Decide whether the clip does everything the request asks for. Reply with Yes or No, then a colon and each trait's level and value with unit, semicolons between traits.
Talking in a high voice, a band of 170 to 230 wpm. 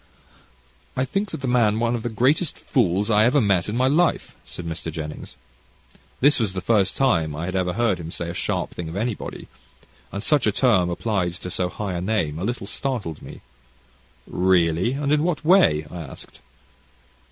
No: low, 105 Hz; average, 195 wpm